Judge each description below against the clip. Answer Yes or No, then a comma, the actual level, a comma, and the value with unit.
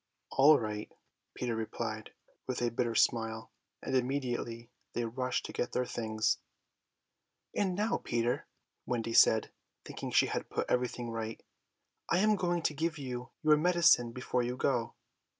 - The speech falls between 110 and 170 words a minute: Yes, average, 150 wpm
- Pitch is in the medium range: No, low, 125 Hz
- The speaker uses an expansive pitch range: No, average, 3.7 semitones